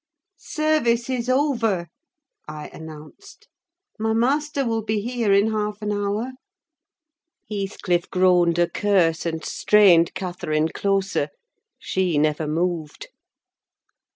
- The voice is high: Yes, high, 200 Hz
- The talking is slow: Yes, slow, 105 wpm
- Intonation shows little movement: No, average, 5.1 semitones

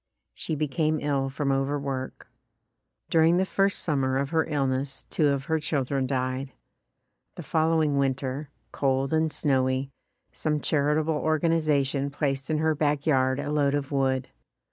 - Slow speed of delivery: No, average, 145 wpm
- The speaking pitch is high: No, medium, 140 Hz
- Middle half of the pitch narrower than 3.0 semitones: Yes, narrow, 2.5 semitones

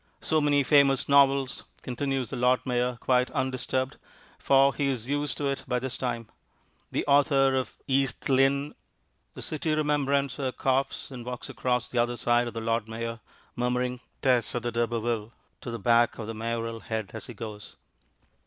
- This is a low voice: Yes, low, 125 Hz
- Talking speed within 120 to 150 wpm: No, average, 180 wpm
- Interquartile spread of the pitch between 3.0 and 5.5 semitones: No, narrow, 2.6 semitones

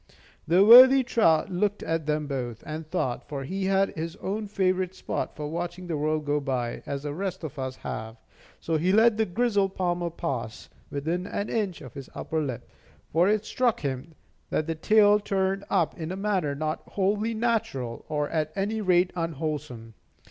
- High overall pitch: No, medium, 170 Hz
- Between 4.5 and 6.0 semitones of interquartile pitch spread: Yes, average, 5.1 semitones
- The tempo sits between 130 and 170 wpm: No, average, 185 wpm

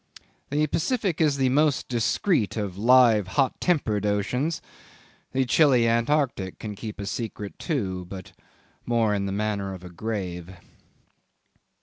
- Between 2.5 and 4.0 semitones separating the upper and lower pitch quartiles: No, wide, 5.5 semitones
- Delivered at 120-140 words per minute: Yes, slow, 135 wpm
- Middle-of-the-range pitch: No, low, 115 Hz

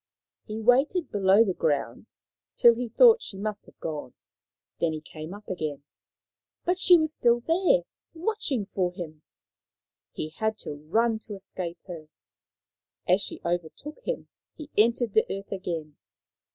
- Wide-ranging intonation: Yes, wide, 6.5 semitones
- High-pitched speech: Yes, high, 205 Hz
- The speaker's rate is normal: Yes, average, 150 wpm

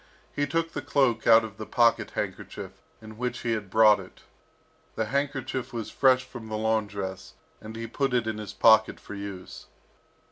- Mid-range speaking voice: No, low, 110 Hz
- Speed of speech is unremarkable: Yes, average, 180 wpm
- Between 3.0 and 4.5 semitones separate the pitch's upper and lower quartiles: No, narrow, 2.6 semitones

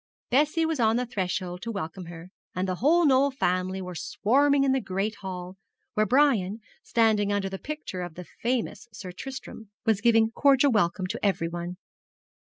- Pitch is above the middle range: Yes, high, 210 Hz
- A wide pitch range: Yes, wide, 6.1 semitones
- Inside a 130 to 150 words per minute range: No, average, 170 wpm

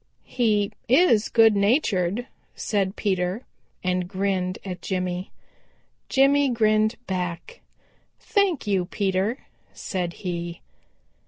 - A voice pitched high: Yes, high, 200 Hz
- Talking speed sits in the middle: No, slow, 95 wpm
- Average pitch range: Yes, average, 4.0 semitones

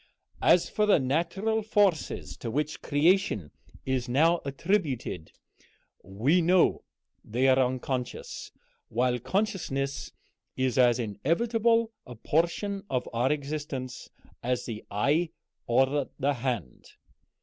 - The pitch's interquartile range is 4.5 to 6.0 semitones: Yes, wide, 5.6 semitones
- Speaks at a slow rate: Yes, slow, 115 wpm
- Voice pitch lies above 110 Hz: Yes, medium, 140 Hz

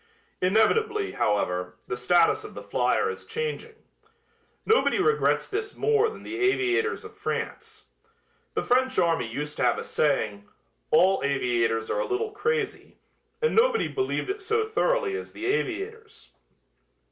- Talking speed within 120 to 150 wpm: Yes, average, 145 wpm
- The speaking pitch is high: Yes, very high, 395 Hz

